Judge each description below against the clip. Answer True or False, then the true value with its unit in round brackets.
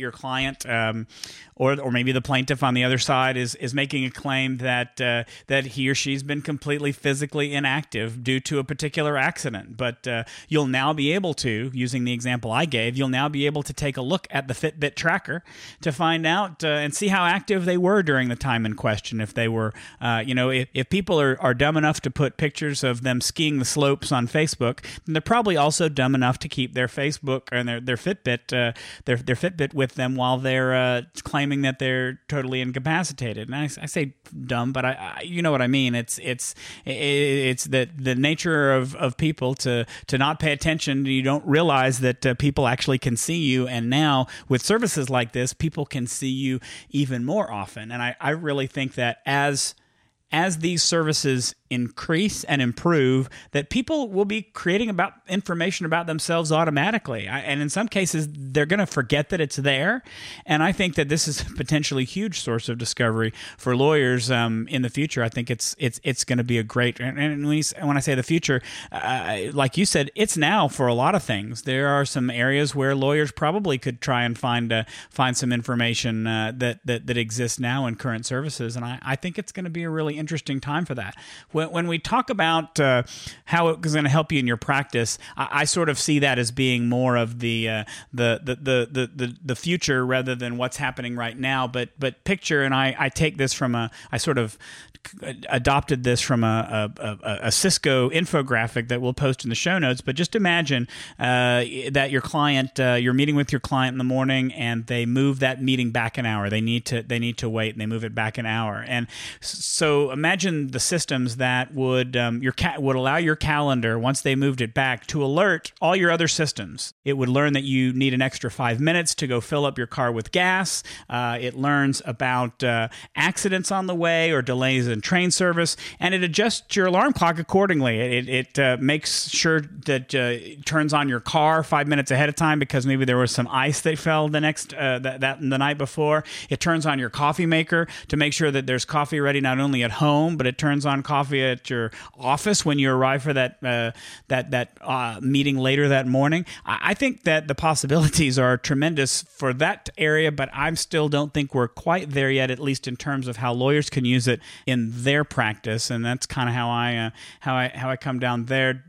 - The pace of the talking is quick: True (220 wpm)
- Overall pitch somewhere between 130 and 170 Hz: True (135 Hz)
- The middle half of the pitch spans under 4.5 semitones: True (3.5 semitones)